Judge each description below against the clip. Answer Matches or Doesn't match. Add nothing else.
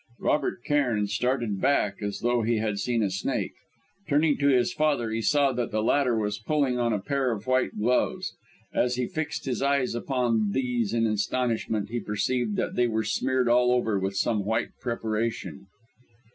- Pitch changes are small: Doesn't match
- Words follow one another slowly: Doesn't match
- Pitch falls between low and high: Doesn't match